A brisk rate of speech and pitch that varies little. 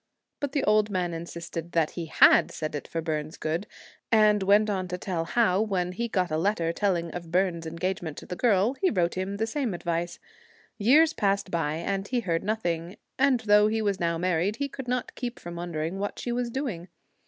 No: fast, 210 wpm; average, 4.3 semitones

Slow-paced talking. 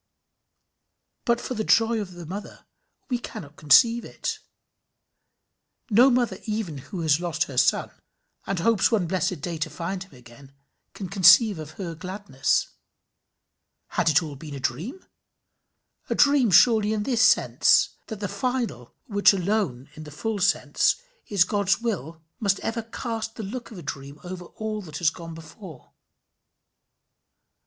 No: average, 155 wpm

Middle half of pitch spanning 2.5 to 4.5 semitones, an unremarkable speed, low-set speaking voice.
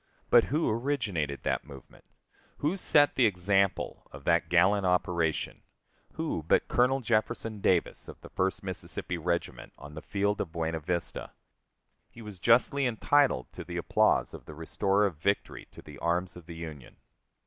No: wide, 5.6 semitones; average, 160 wpm; very low, 95 Hz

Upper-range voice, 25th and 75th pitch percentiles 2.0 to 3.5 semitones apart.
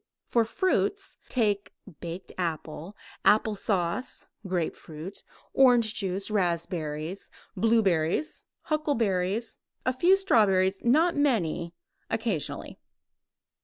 No: high, 200 Hz; wide, 5.5 semitones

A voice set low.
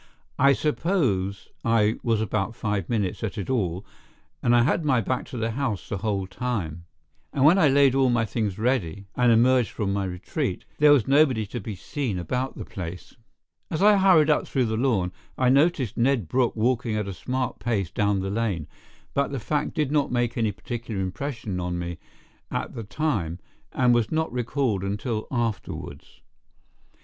Yes: low, 115 Hz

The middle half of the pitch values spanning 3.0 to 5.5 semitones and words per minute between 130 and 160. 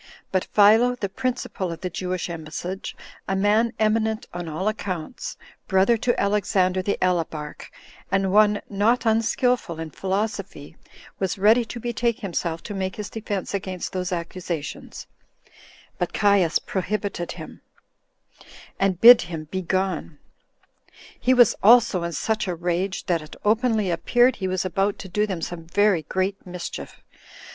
Yes: average, 3.4 semitones; average, 145 wpm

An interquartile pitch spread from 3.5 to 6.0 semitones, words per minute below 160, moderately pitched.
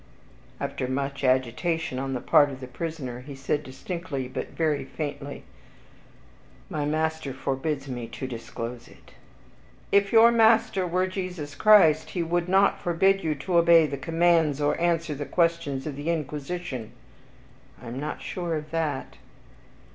Yes: average, 4.0 semitones; average, 150 wpm; medium, 150 Hz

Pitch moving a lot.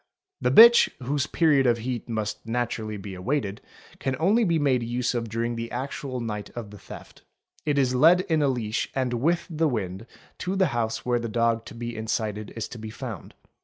No: average, 3.9 semitones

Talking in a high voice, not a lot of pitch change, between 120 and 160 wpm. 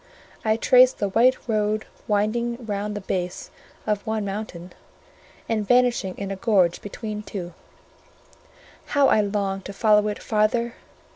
Yes: high, 210 Hz; narrow, 2.3 semitones; average, 140 wpm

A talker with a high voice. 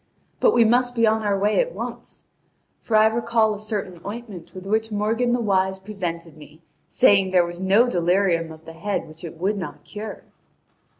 Yes: high, 200 Hz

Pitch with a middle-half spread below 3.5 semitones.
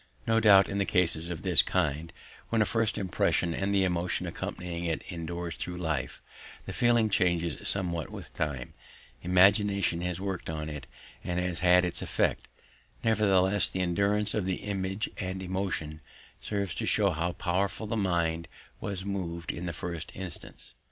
Yes: average, 2.8 semitones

